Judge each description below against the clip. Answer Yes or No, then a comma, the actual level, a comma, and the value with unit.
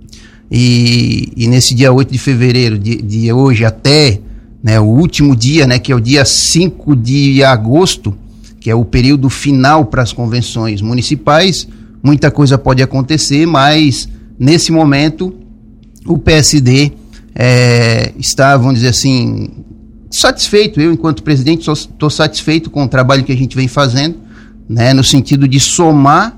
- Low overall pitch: Yes, low, 130 Hz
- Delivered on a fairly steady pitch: No, average, 4.0 semitones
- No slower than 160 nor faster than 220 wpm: No, average, 150 wpm